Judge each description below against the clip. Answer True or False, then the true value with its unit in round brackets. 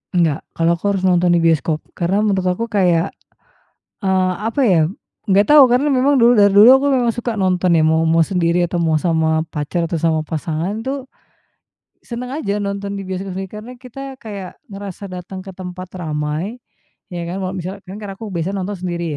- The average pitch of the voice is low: False (185 Hz)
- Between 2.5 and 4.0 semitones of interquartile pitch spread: True (3.6 semitones)